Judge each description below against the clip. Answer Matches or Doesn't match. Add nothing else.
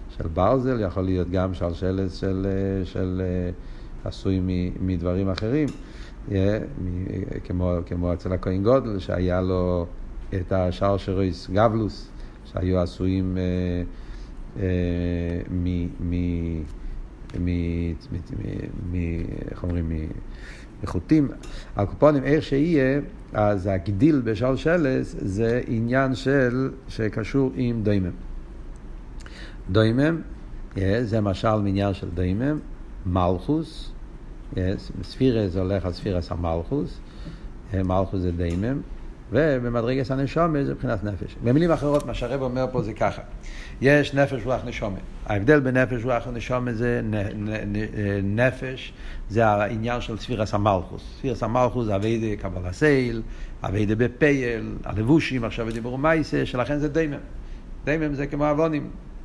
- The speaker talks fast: Doesn't match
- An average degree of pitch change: Doesn't match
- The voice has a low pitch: Matches